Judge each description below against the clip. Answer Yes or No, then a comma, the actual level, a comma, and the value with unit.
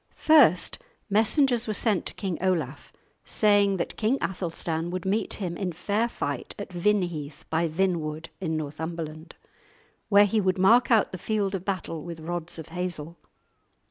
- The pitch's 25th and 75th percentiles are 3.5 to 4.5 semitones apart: Yes, average, 3.9 semitones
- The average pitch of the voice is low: No, medium, 185 Hz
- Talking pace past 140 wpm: Yes, average, 155 wpm